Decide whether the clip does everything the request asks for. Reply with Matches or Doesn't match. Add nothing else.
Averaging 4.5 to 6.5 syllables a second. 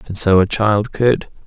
Doesn't match